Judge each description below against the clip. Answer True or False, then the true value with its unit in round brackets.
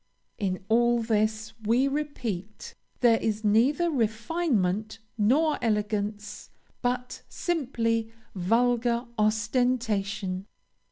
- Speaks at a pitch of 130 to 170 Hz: False (225 Hz)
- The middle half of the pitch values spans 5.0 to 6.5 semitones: False (2.8 semitones)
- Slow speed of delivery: True (80 wpm)